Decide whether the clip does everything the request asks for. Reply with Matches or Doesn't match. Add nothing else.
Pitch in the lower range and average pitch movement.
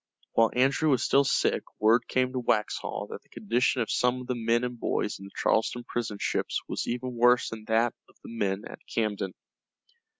Doesn't match